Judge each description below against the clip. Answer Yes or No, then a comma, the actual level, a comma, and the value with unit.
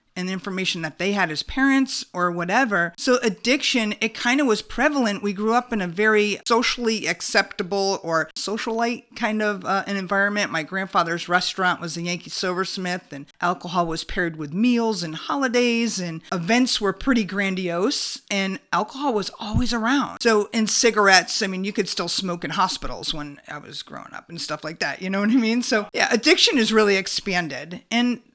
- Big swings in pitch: No, average, 4.5 semitones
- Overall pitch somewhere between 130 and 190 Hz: No, high, 200 Hz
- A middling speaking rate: Yes, average, 190 wpm